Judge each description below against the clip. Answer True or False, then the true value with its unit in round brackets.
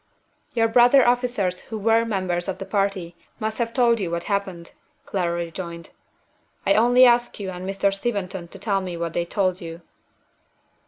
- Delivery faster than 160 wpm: True (170 wpm)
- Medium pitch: False (195 Hz)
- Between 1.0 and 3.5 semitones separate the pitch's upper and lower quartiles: False (4.5 semitones)